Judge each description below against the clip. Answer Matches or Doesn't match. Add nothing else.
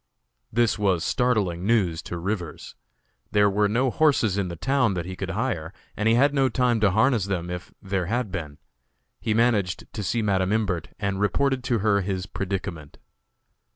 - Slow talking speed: Doesn't match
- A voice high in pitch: Doesn't match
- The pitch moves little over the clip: Doesn't match